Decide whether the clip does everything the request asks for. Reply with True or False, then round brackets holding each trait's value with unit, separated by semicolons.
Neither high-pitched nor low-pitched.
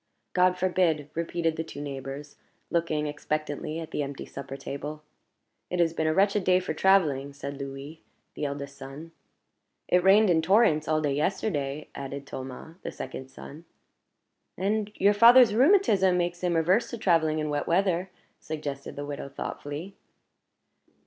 True (160 Hz)